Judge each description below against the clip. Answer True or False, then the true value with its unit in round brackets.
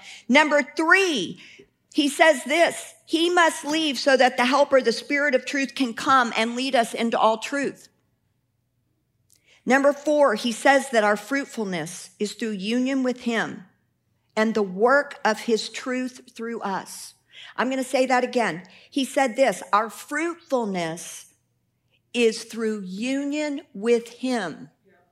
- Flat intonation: False (4.1 semitones)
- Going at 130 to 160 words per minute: True (145 wpm)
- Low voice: False (250 Hz)